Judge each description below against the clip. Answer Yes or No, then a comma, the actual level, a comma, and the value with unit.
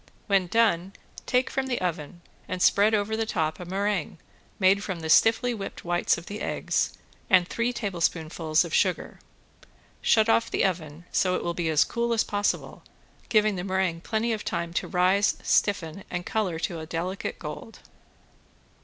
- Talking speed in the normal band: Yes, average, 170 wpm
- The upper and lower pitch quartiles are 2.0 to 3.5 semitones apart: No, average, 3.9 semitones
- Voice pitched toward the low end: No, medium, 185 Hz